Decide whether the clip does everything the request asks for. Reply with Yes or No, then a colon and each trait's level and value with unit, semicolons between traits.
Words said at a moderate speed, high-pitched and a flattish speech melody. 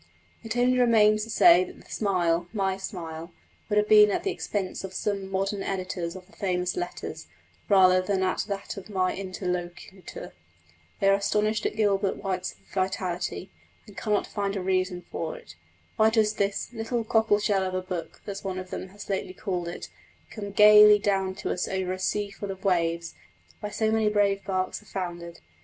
Yes: average, 185 wpm; high, 195 Hz; narrow, 2.3 semitones